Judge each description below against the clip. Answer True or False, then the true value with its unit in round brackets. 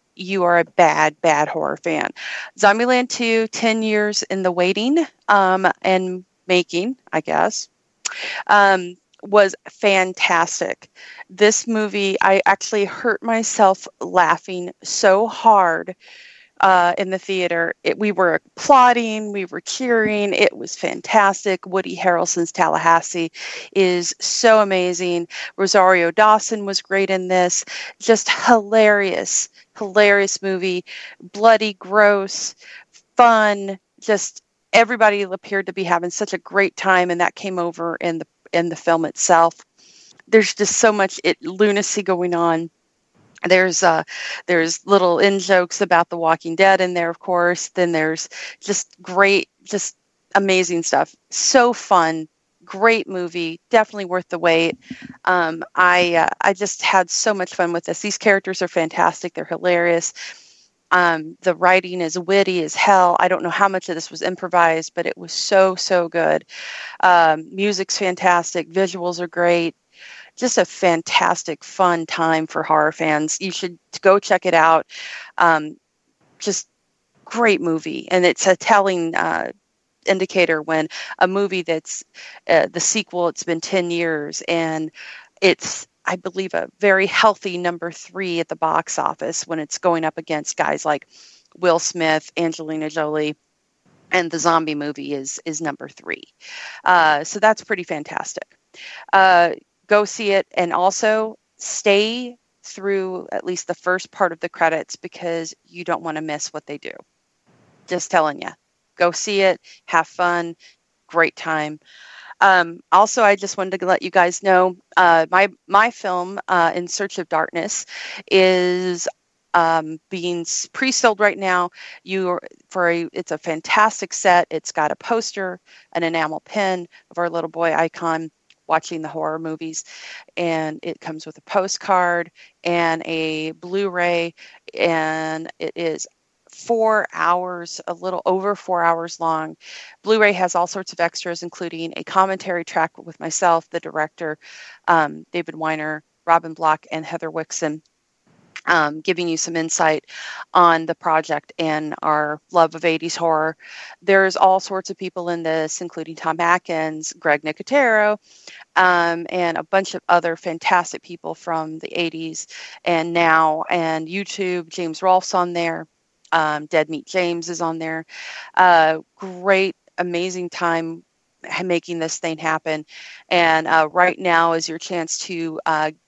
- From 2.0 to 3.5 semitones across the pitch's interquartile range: True (2.9 semitones)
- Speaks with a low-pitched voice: False (180 Hz)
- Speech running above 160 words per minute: False (150 wpm)